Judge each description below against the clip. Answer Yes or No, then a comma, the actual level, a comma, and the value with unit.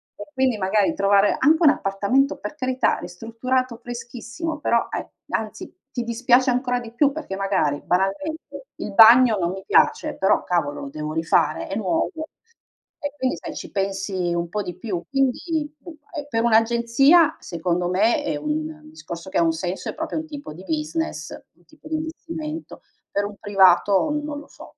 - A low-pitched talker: No, high, 225 Hz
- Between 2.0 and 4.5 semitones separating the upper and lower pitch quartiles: No, wide, 7.2 semitones